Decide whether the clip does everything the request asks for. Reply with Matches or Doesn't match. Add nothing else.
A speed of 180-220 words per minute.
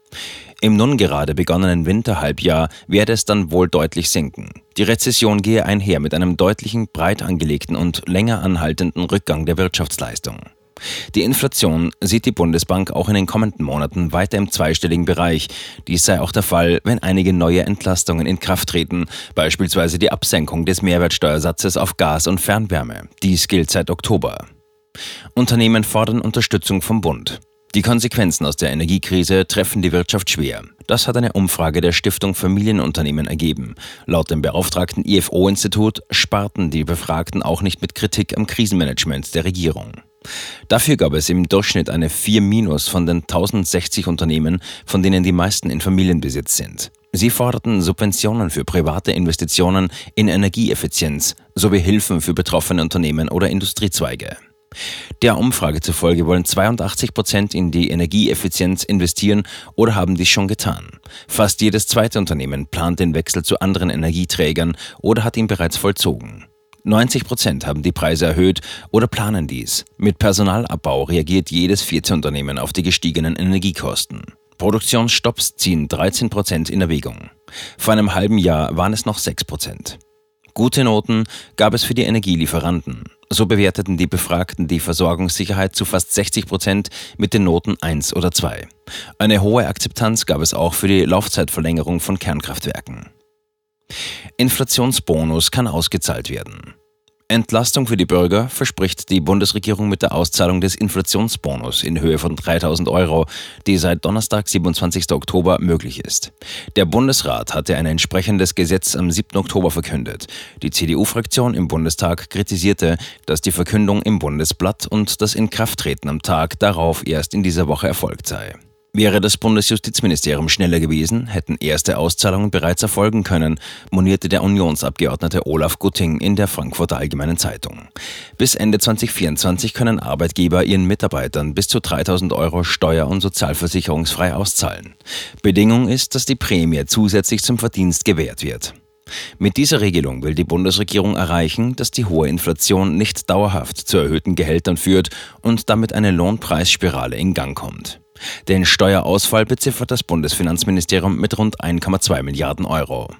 Doesn't match